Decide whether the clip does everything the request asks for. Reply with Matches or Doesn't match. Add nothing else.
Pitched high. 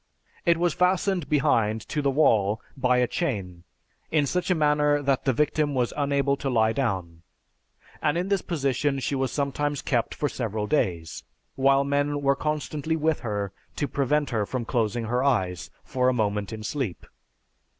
Doesn't match